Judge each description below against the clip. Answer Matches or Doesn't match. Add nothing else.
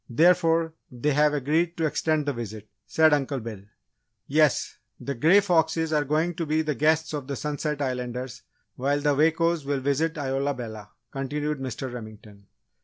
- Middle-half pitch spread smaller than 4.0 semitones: Matches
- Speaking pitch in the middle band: Matches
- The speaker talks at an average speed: Matches